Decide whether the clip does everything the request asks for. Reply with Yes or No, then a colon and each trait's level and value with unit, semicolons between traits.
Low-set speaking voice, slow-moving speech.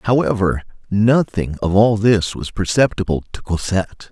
Yes: low, 100 Hz; slow, 130 wpm